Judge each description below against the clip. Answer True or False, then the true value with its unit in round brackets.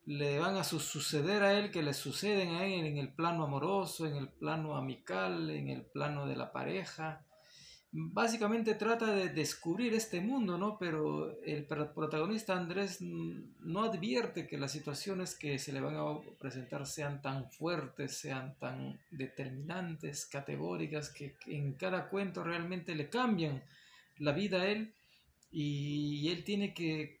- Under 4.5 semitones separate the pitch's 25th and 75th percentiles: False (4.8 semitones)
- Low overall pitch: False (160 Hz)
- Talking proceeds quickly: False (150 wpm)